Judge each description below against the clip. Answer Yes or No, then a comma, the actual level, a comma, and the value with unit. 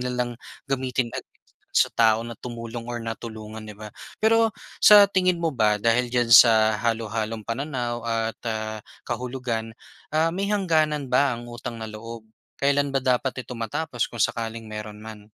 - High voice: No, low, 120 Hz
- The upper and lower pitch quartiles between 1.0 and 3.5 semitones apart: Yes, average, 3.2 semitones